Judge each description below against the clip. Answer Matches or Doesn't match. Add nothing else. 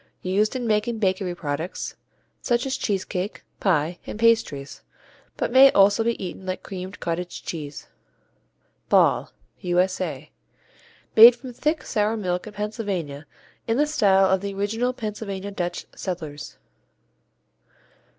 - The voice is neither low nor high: Doesn't match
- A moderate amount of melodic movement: Matches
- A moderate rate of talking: Doesn't match